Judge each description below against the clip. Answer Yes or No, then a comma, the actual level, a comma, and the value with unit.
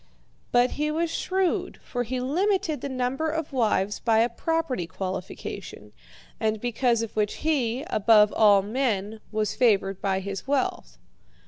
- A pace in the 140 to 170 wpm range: Yes, average, 145 wpm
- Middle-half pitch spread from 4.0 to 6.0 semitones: Yes, average, 5.3 semitones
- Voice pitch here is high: Yes, high, 240 Hz